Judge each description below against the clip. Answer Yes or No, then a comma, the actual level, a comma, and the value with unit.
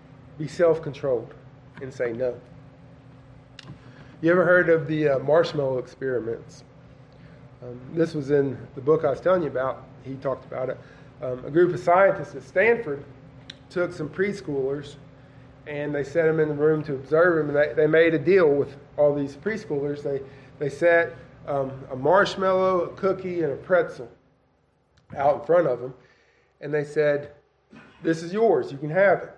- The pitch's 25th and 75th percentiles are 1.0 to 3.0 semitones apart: No, average, 3.5 semitones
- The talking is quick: No, average, 170 wpm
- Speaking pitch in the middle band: Yes, medium, 145 Hz